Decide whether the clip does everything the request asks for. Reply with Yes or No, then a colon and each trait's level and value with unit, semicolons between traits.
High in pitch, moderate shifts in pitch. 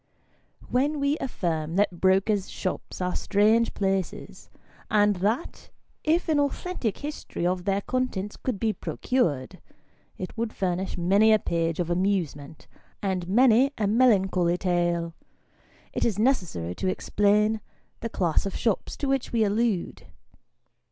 Yes: high, 200 Hz; average, 4.4 semitones